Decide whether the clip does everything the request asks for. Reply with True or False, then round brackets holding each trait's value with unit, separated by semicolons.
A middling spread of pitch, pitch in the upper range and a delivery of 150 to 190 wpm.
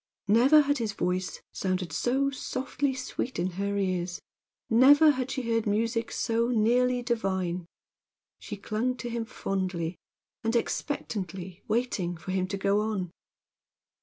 False (4.9 semitones; 220 Hz; 135 wpm)